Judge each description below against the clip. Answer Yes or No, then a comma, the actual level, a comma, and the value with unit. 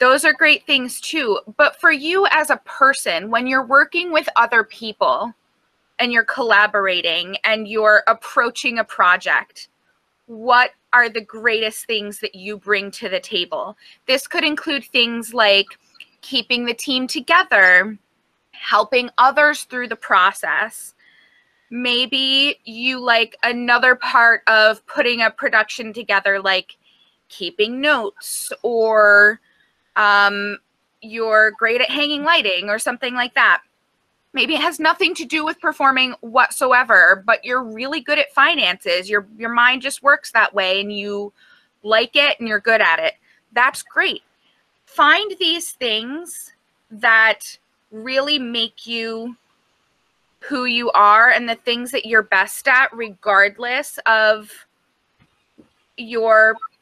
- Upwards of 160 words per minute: No, slow, 135 wpm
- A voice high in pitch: Yes, high, 240 Hz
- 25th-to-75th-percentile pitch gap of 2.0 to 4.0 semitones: No, average, 4.7 semitones